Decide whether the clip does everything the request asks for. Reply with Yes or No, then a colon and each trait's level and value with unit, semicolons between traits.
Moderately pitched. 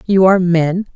Yes: medium, 180 Hz